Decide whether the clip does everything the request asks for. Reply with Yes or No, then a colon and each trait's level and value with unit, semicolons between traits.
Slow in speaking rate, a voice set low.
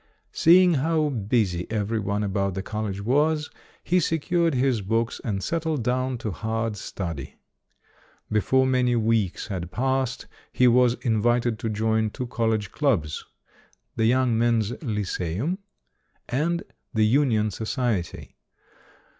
Yes: slow, 130 wpm; low, 115 Hz